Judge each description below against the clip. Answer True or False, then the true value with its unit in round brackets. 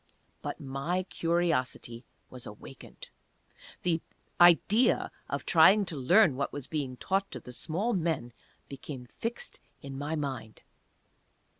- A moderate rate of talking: False (125 wpm)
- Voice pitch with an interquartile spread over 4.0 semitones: True (5.2 semitones)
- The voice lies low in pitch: False (150 Hz)